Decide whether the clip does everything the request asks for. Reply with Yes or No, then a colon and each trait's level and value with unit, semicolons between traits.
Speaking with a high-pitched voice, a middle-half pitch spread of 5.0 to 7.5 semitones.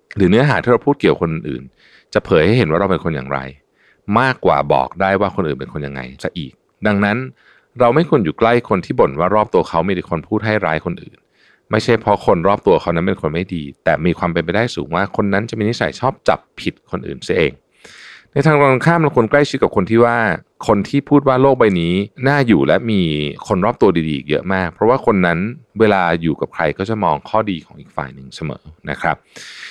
No: low, 100 Hz; wide, 5.6 semitones